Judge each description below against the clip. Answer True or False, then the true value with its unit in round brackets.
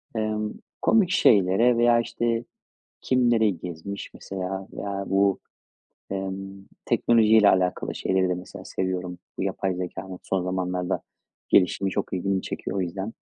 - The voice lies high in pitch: False (95 Hz)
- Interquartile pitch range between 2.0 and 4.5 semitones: True (2.8 semitones)